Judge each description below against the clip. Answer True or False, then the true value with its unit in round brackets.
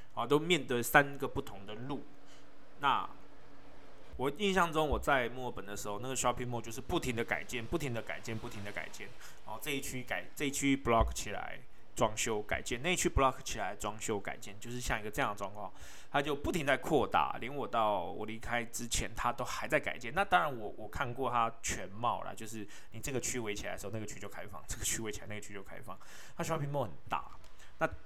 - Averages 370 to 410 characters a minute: True (380 characters per minute)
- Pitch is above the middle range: False (120 Hz)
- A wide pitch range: False (4.5 semitones)